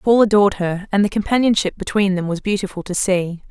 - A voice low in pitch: No, high, 195 Hz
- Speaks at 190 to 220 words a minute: Yes, fast, 205 wpm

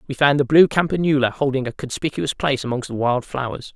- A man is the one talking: Yes, male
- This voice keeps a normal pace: No, fast, 210 wpm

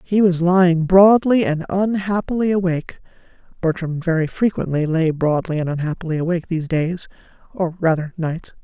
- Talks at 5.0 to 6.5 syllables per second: Yes, 5.3 syllables/s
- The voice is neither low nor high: Yes, medium, 175 Hz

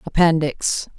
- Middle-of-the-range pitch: Yes, medium, 160 Hz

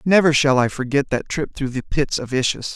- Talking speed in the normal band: No, fast, 240 wpm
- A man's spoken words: Yes, male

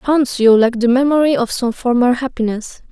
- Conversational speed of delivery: Yes, average, 185 wpm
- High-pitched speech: Yes, very high, 250 Hz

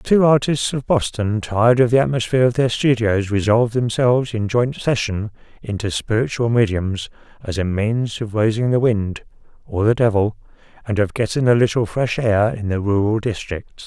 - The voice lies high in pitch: No, low, 115 Hz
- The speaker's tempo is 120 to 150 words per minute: No, average, 165 wpm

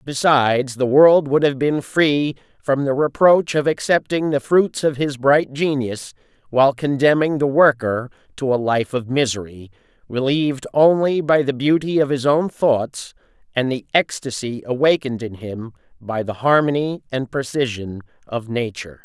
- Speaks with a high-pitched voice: No, low, 135 Hz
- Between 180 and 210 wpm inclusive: No, average, 155 wpm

